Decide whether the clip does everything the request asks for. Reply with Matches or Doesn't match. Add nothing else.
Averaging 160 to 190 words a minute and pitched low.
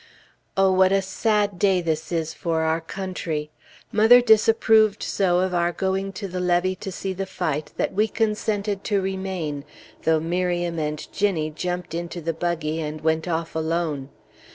Doesn't match